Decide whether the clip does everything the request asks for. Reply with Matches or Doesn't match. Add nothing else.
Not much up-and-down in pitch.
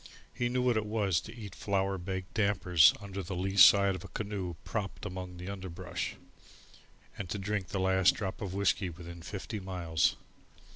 Matches